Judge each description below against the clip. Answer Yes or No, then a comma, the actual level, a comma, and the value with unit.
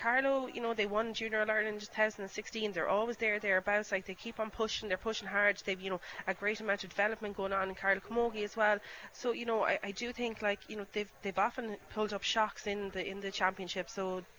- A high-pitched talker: Yes, high, 210 Hz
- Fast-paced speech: Yes, fast, 255 wpm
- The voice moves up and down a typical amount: No, narrow, 2.2 semitones